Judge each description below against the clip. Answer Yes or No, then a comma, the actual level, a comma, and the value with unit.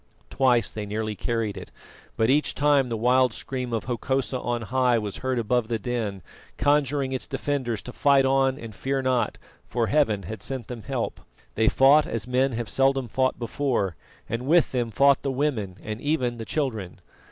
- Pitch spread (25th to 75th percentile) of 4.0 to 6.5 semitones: No, average, 3.1 semitones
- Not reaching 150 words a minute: No, average, 185 wpm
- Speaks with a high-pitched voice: No, low, 125 Hz